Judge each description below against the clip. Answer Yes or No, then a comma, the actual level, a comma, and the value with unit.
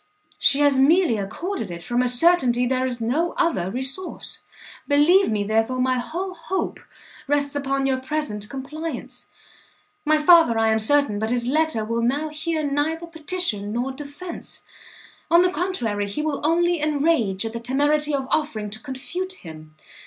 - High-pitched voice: Yes, very high, 280 Hz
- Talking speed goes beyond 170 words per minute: No, average, 160 wpm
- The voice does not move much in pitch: No, average, 5.3 semitones